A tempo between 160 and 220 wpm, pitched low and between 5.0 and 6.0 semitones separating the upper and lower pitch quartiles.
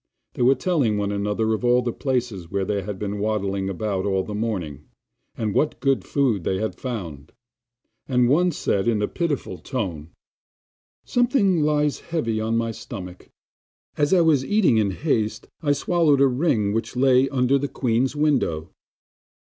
Yes: average, 165 wpm; low, 115 Hz; wide, 5.6 semitones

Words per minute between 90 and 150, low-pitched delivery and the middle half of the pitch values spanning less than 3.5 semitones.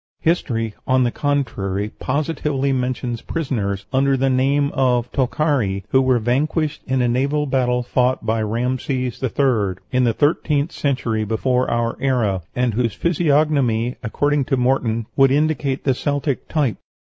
Yes: average, 145 wpm; low, 130 Hz; average, 3.1 semitones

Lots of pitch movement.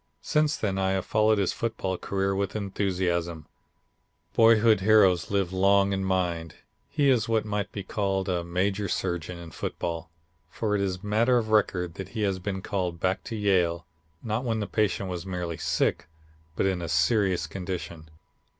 No: average, 3.0 semitones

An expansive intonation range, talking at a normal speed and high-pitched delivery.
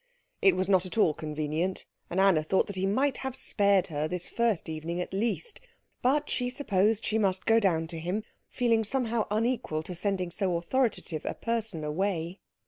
No: average, 4.9 semitones; average, 190 wpm; high, 195 Hz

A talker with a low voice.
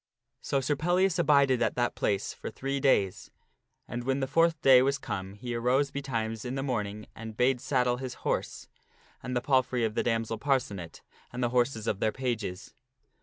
Yes: low, 125 Hz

